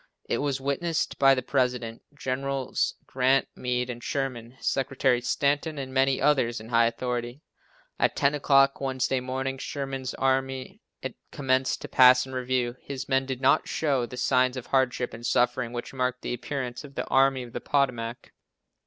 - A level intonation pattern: Yes, narrow, 1.6 semitones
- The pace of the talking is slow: No, average, 165 wpm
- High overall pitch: No, low, 130 Hz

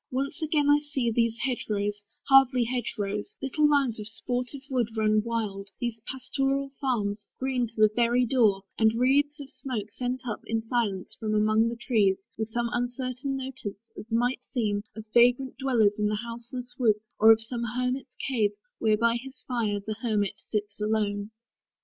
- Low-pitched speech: No, high, 235 Hz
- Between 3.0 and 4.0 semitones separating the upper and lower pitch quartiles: Yes, average, 3.3 semitones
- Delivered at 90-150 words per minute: No, average, 175 wpm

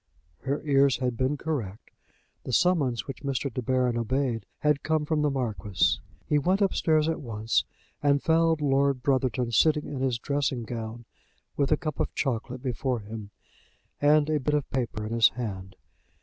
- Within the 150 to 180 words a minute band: Yes, average, 170 wpm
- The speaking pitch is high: No, low, 135 Hz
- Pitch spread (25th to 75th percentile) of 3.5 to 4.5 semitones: Yes, average, 3.8 semitones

